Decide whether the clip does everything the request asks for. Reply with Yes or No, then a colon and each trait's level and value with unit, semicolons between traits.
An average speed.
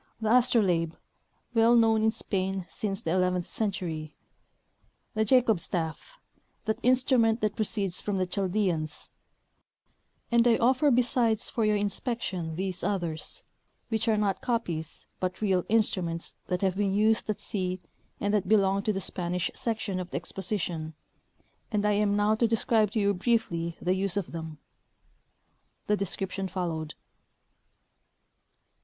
Yes: average, 145 wpm